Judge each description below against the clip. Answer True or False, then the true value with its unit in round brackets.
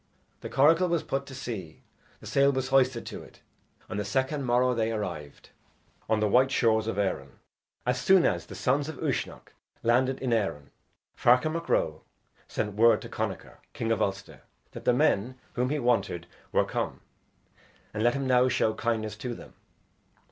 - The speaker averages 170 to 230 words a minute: True (175 wpm)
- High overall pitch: False (120 Hz)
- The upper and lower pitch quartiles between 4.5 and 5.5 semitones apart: False (3.8 semitones)